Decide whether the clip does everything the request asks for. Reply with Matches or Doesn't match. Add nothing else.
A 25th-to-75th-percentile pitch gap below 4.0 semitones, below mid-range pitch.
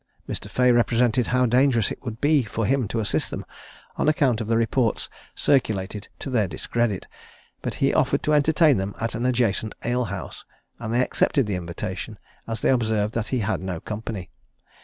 Matches